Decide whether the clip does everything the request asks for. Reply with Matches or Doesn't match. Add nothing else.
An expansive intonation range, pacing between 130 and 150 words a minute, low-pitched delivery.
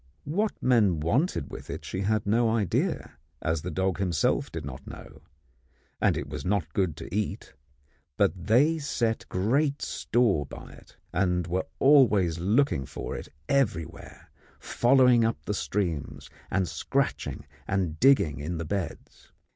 Matches